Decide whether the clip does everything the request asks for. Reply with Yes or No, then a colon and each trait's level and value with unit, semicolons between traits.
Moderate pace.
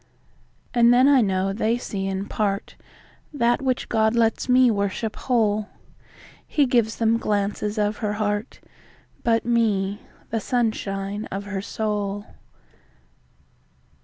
No: slow, 110 wpm